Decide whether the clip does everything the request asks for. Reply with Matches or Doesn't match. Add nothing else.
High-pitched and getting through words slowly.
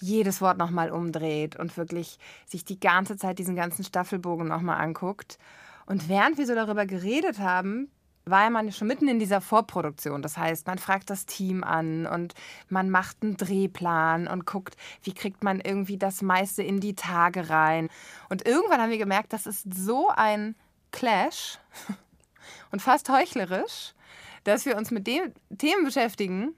Doesn't match